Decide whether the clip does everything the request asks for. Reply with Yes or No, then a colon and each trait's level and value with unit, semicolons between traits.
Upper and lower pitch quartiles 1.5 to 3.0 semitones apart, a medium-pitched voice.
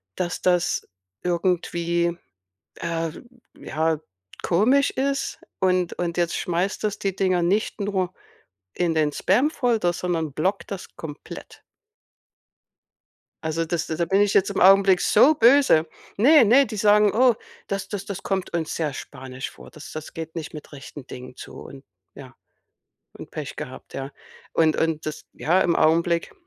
No: average, 3.8 semitones; medium, 175 Hz